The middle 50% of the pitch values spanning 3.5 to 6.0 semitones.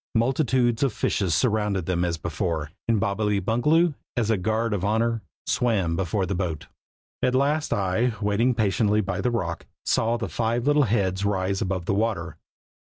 Yes: average, 3.9 semitones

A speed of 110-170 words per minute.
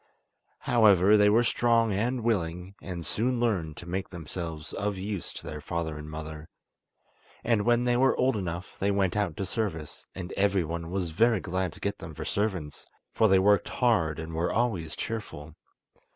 No: average, 180 wpm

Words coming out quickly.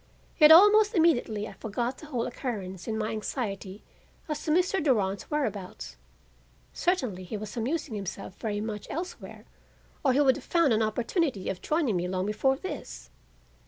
No: average, 160 wpm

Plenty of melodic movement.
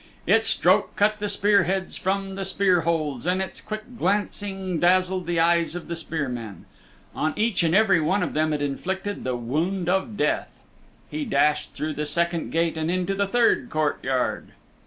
No: average, 3.9 semitones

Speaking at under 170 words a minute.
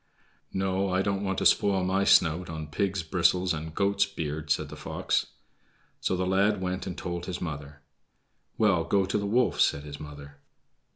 No: average, 180 wpm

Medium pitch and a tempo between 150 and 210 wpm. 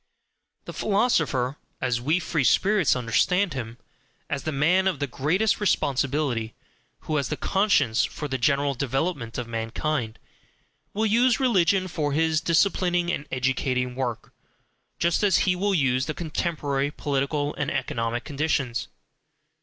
No: medium, 145 Hz; average, 140 wpm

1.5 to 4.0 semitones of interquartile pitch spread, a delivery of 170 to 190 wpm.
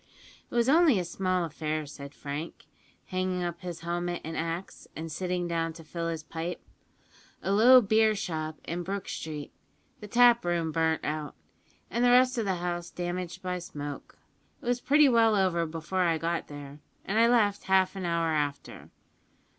Yes: average, 3.6 semitones; average, 175 wpm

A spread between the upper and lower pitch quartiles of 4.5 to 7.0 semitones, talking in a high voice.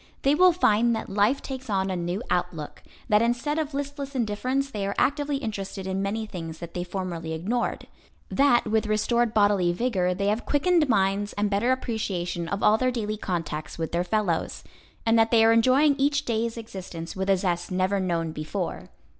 Yes: average, 4.8 semitones; high, 210 Hz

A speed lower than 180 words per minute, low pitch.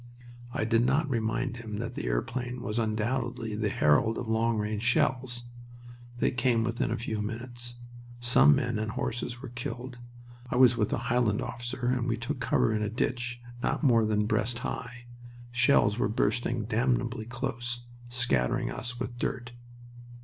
Yes: average, 165 wpm; low, 120 Hz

